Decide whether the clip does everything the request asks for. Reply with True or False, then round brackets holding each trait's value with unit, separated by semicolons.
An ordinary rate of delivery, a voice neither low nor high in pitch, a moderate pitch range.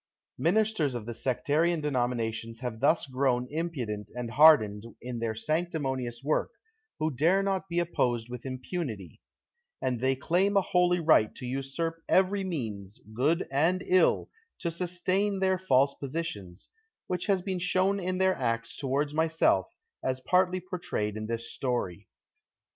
False (145 wpm; 145 Hz; 6.7 semitones)